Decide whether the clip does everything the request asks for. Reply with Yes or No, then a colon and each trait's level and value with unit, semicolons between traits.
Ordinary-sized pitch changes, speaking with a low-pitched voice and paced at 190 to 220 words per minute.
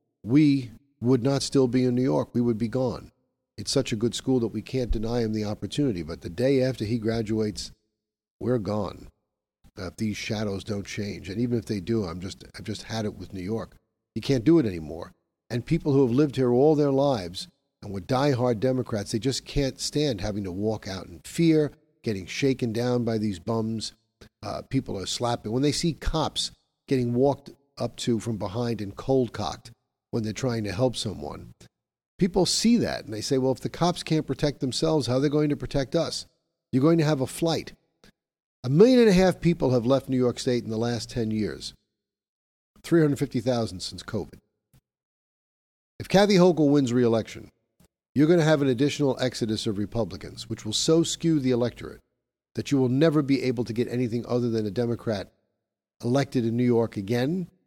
Yes: average, 4.2 semitones; low, 120 Hz; average, 200 wpm